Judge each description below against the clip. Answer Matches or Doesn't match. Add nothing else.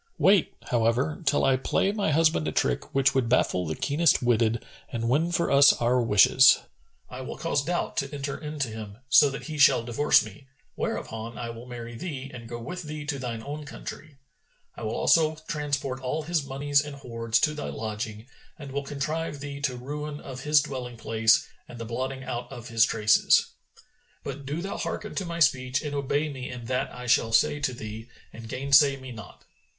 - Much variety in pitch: Doesn't match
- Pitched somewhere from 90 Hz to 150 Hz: Matches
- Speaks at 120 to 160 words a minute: Doesn't match